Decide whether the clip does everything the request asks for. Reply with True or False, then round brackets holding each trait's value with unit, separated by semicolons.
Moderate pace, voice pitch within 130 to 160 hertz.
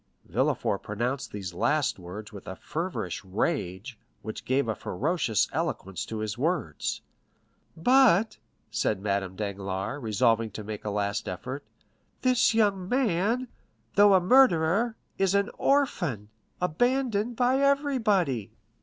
False (125 wpm; 140 Hz)